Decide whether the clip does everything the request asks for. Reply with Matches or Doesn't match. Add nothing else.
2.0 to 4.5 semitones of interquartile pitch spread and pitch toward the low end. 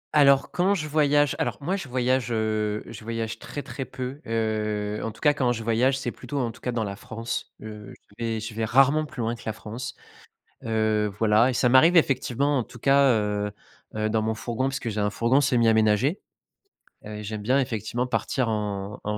Matches